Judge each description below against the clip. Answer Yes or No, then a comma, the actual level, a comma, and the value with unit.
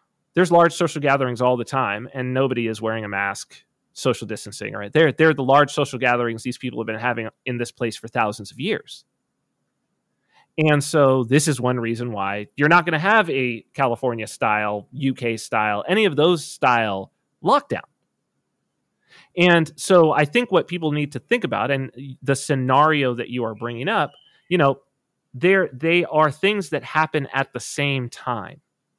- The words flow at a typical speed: Yes, average, 180 wpm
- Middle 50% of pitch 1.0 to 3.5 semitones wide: No, average, 4.6 semitones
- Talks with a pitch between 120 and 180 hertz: Yes, low, 135 Hz